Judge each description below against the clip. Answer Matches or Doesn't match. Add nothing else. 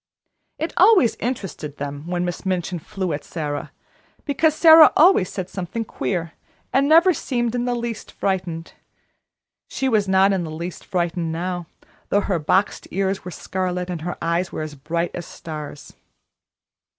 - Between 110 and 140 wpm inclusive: Doesn't match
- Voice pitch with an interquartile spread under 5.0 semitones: Doesn't match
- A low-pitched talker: Doesn't match